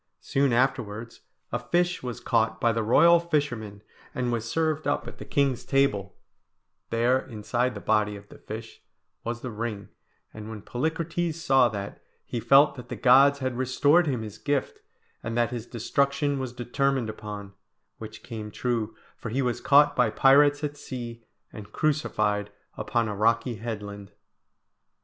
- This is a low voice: Yes, low, 120 Hz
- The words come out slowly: No, average, 160 wpm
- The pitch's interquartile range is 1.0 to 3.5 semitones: No, average, 4.1 semitones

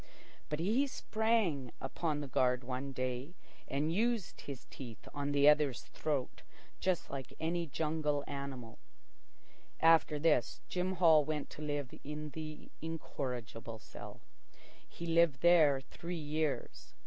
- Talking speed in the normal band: No, slow, 130 wpm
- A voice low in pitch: No, medium, 150 Hz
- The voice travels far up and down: No, average, 3.5 semitones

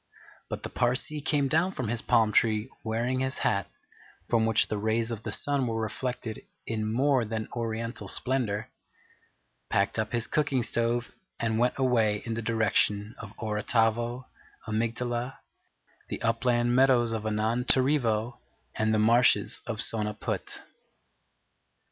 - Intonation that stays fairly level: Yes, narrow, 2.2 semitones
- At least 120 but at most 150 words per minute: Yes, slow, 135 wpm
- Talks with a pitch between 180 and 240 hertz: No, low, 115 Hz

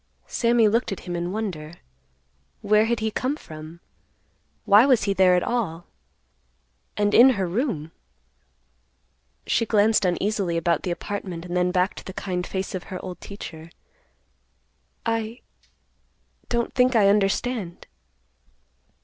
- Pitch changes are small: No, average, 4.0 semitones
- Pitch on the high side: Yes, high, 200 Hz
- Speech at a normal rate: No, slow, 130 wpm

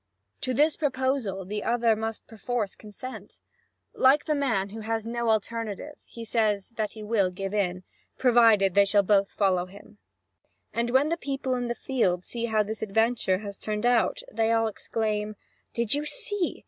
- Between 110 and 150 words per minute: No, average, 175 wpm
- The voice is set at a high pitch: Yes, high, 225 Hz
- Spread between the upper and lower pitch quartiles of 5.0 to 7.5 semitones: No, average, 3.1 semitones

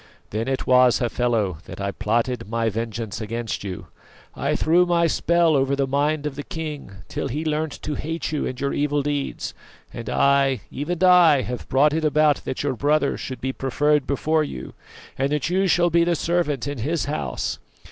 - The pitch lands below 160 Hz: Yes, medium, 140 Hz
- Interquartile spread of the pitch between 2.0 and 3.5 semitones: No, average, 4.0 semitones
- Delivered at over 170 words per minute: Yes, average, 190 wpm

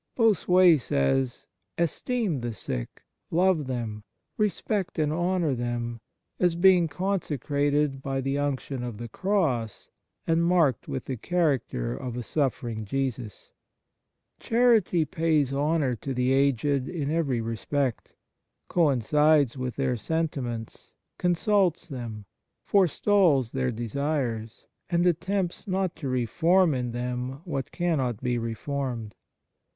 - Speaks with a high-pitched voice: No, medium, 140 Hz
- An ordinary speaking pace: No, slow, 120 wpm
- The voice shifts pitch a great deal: Yes, wide, 5.8 semitones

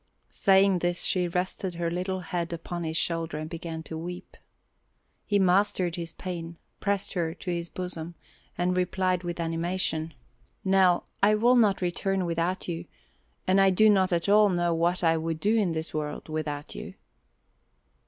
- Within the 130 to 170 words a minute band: Yes, average, 165 wpm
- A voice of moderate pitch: Yes, medium, 175 Hz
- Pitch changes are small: Yes, narrow, 2.2 semitones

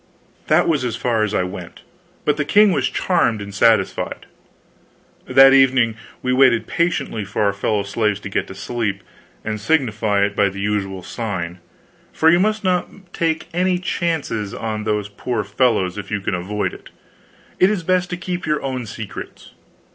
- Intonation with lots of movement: Yes, wide, 7.8 semitones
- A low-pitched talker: Yes, low, 115 Hz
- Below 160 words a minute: No, average, 175 wpm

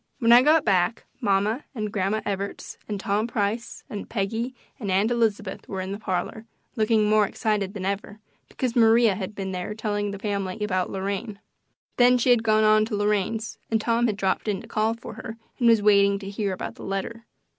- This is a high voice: Yes, high, 210 Hz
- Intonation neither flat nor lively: No, narrow, 2.3 semitones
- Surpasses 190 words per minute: Yes, average, 200 wpm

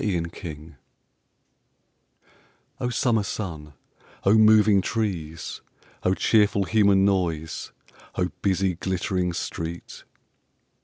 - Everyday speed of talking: No, slow, 80 wpm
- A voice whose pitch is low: Yes, very low, 95 Hz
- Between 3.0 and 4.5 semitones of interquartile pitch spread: Yes, average, 3.5 semitones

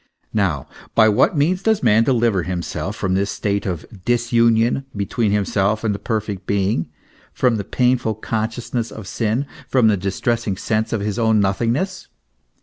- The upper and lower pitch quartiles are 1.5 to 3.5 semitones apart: Yes, average, 2.9 semitones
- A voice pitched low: Yes, low, 110 Hz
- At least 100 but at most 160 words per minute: Yes, average, 155 wpm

